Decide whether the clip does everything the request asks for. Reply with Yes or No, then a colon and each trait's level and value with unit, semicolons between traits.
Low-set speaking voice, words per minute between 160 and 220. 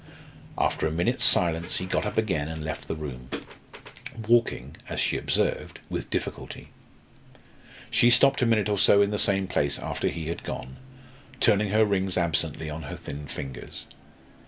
Yes: very low, 85 Hz; average, 165 wpm